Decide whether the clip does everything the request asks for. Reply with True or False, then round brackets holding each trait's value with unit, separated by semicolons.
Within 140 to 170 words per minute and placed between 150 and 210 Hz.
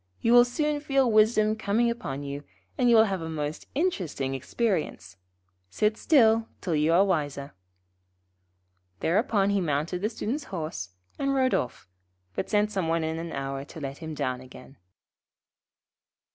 True (155 wpm; 185 Hz)